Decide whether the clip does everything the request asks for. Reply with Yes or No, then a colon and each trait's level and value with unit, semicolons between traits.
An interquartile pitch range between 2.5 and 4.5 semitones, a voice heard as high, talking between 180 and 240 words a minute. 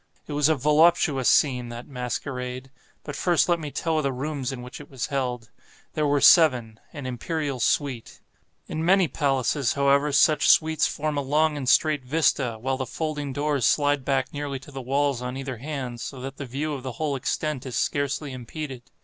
No: average, 2.8 semitones; medium, 140 Hz; average, 190 wpm